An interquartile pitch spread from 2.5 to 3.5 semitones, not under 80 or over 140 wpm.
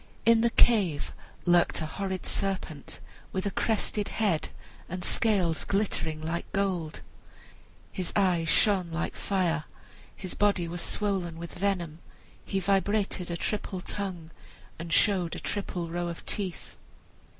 Yes: average, 3.0 semitones; slow, 135 wpm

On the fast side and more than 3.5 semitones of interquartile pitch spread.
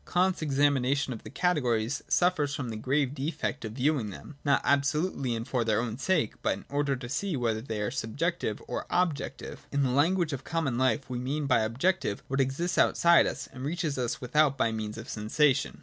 Yes: fast, 215 wpm; average, 4.0 semitones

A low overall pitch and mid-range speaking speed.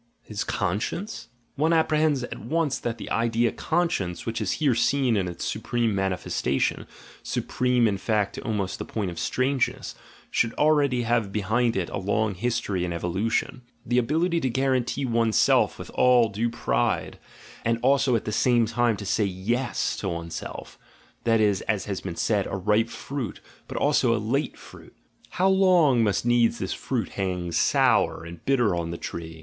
Yes: low, 115 Hz; average, 185 wpm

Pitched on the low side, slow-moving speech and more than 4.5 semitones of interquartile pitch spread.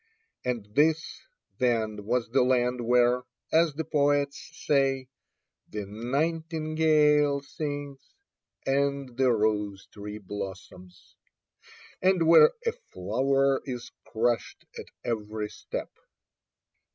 Yes: low, 130 Hz; slow, 100 wpm; average, 4.9 semitones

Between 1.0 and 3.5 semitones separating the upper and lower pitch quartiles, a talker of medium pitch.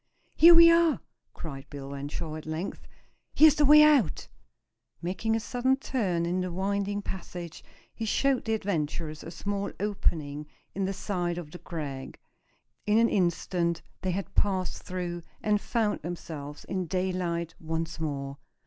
No: average, 4.4 semitones; medium, 180 Hz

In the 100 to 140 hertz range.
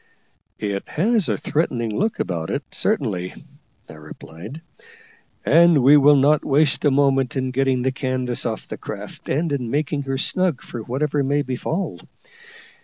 Yes: low, 135 Hz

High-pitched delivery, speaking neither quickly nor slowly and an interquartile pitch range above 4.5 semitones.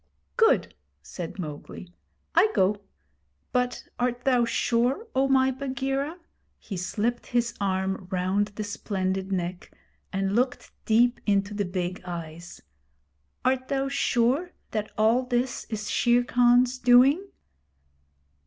No: high, 230 Hz; slow, 125 wpm; average, 4.9 semitones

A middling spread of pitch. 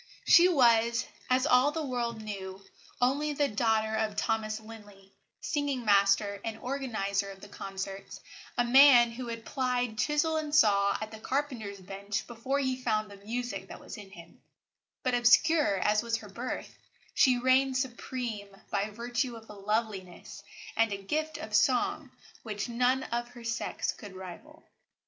Yes: average, 3.9 semitones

